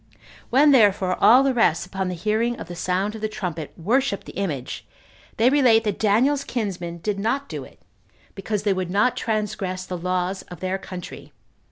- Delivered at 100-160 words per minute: No, average, 185 wpm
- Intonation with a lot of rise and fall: No, average, 3.6 semitones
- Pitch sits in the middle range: No, high, 200 Hz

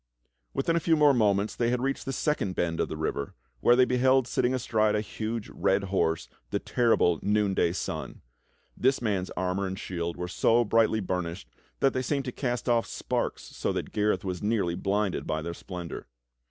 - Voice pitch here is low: Yes, low, 105 Hz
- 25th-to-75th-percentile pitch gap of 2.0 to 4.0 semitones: No, average, 5.1 semitones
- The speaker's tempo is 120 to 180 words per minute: No, average, 190 wpm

